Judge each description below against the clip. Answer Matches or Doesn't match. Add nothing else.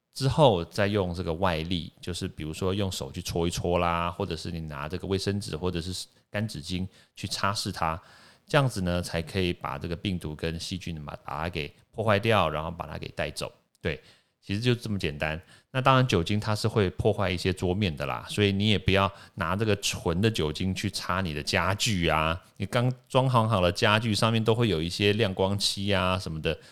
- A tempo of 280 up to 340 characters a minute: Matches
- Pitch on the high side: Doesn't match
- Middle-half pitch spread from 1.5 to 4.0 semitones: Matches